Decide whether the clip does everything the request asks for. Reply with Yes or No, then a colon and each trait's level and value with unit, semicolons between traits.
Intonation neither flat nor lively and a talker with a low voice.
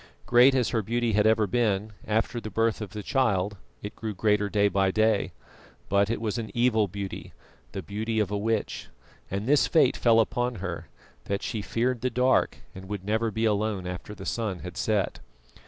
No: narrow, 2.3 semitones; low, 110 Hz